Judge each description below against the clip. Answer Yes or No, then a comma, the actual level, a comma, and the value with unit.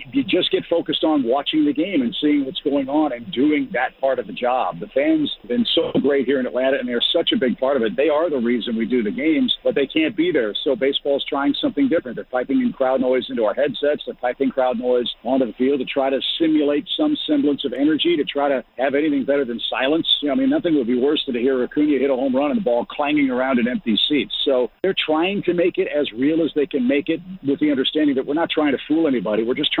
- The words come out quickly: Yes, fast, 275 wpm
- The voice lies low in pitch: No, medium, 150 Hz